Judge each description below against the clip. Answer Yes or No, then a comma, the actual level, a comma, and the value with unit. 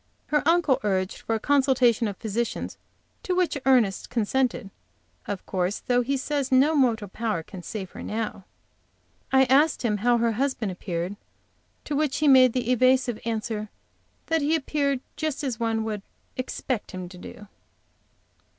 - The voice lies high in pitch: Yes, high, 240 Hz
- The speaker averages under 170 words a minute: Yes, average, 160 wpm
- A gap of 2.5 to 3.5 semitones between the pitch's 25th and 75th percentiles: No, average, 4.3 semitones